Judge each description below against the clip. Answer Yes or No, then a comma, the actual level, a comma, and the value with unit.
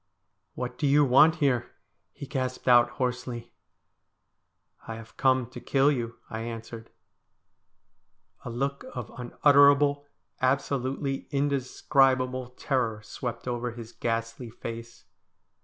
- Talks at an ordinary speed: No, slow, 125 wpm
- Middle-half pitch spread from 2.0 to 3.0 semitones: Yes, average, 2.7 semitones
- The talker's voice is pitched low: Yes, low, 125 Hz